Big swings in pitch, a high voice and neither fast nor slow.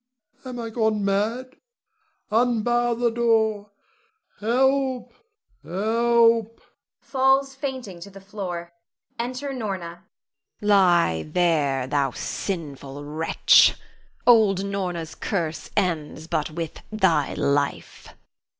No: wide, 5.8 semitones; high, 200 Hz; slow, 95 wpm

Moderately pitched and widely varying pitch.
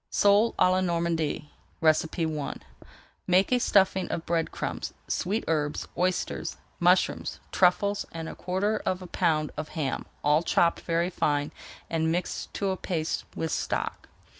No: medium, 170 Hz; average, 2.8 semitones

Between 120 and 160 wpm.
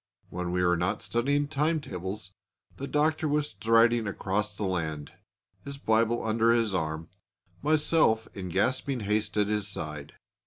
Yes: average, 150 wpm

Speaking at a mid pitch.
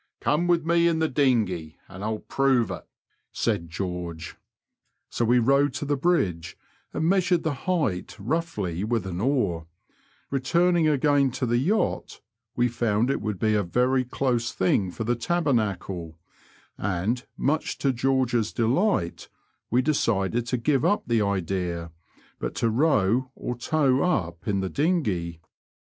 No: low, 120 Hz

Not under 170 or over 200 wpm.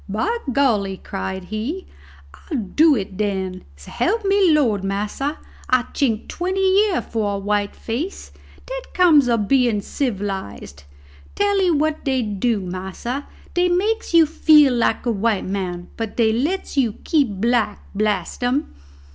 No: average, 145 wpm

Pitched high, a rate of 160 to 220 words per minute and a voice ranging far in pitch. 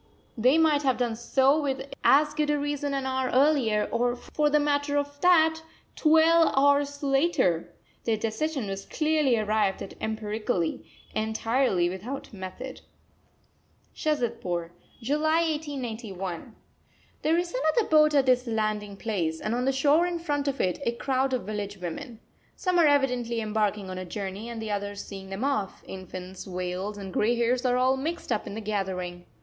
Yes: high, 245 Hz; average, 165 wpm; wide, 5.7 semitones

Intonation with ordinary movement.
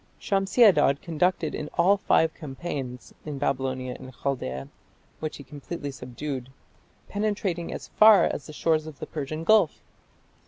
Yes: average, 4.6 semitones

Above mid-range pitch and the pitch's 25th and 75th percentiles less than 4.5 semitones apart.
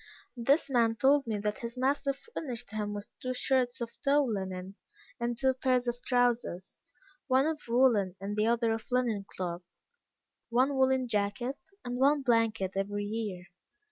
Yes: high, 235 Hz; average, 4.1 semitones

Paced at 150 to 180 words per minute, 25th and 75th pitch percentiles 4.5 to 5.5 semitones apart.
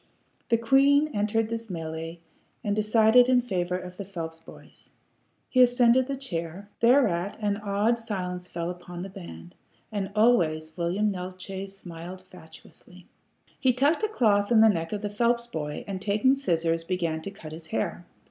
Yes: average, 165 wpm; average, 5.1 semitones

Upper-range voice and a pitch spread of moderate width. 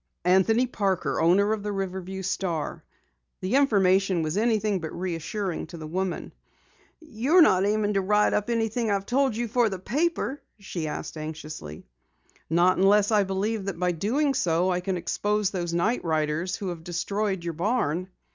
Yes: high, 195 Hz; average, 3.6 semitones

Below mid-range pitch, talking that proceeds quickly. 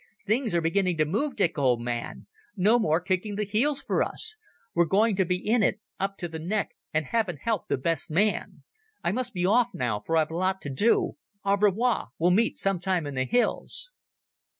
No: high, 190 Hz; fast, 210 wpm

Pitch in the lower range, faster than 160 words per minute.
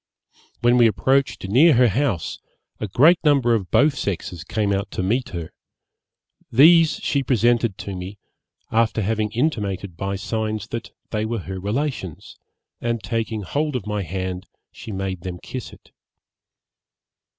No: low, 110 Hz; average, 150 wpm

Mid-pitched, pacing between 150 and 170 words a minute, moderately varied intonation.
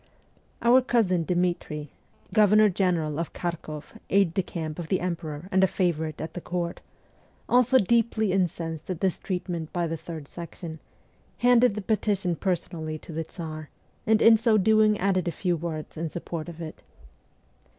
Yes: medium, 175 Hz; average, 160 wpm; average, 3.8 semitones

